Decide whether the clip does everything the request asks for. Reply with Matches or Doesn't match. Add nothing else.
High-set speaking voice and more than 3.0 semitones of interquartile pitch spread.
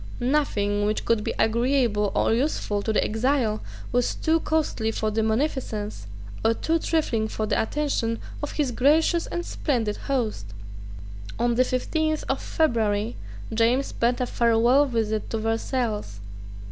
Matches